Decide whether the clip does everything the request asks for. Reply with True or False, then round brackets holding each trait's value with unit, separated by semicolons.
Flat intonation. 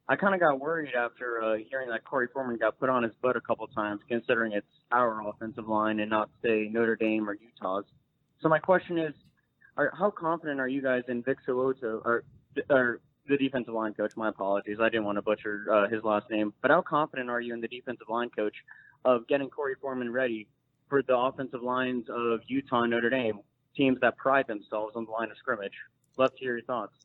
False (3.4 semitones)